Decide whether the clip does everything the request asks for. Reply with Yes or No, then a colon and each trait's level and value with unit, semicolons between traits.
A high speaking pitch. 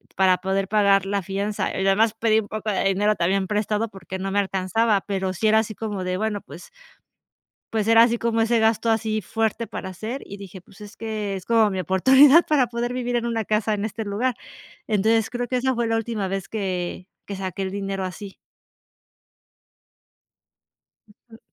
Yes: high, 210 Hz